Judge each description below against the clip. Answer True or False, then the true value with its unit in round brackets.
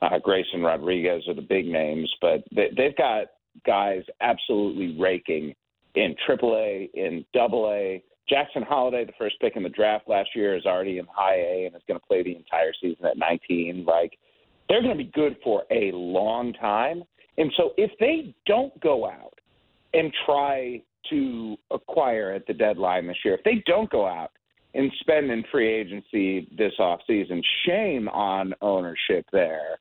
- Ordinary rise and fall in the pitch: False (7.0 semitones)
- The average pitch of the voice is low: True (105 Hz)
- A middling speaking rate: True (175 wpm)